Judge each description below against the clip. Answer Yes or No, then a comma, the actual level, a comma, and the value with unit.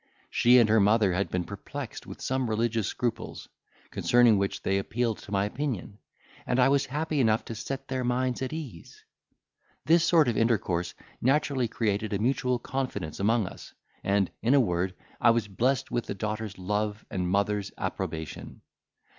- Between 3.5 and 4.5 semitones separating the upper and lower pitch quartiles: Yes, average, 4.2 semitones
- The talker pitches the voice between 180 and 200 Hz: No, low, 115 Hz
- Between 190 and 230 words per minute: No, average, 170 wpm